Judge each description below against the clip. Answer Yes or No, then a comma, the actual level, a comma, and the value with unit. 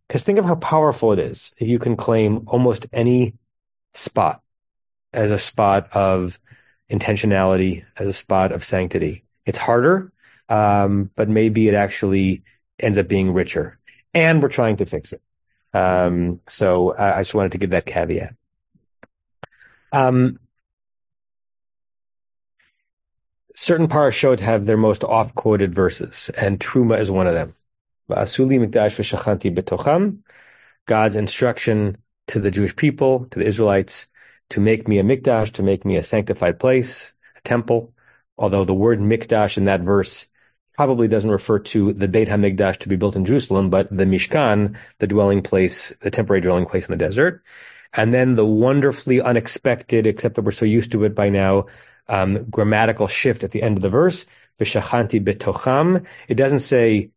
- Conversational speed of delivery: Yes, average, 155 wpm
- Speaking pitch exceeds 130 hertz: No, low, 105 Hz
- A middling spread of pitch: Yes, average, 3.5 semitones